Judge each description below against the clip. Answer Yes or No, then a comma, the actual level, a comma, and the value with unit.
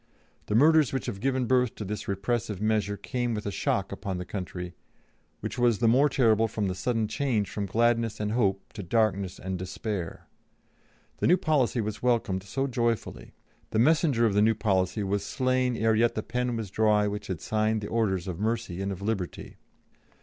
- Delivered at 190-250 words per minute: Yes, average, 195 wpm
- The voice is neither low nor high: No, low, 110 Hz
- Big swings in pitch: No, average, 3.2 semitones